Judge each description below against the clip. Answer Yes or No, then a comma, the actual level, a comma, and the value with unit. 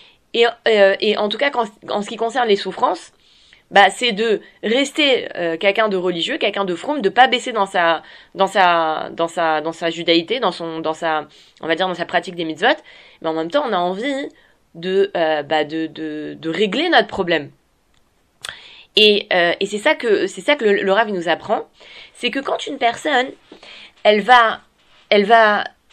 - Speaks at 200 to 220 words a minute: Yes, average, 205 wpm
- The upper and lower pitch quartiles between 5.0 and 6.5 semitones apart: Yes, wide, 5.4 semitones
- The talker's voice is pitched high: Yes, high, 195 Hz